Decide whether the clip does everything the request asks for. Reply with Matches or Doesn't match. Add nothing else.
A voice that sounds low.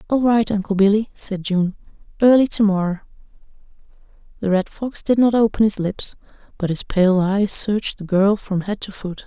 Doesn't match